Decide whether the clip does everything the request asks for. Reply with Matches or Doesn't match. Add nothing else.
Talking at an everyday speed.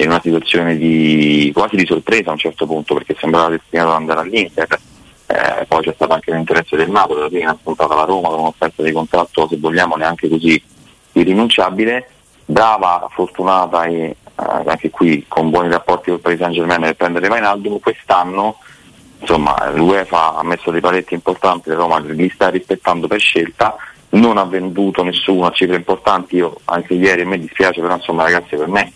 Doesn't match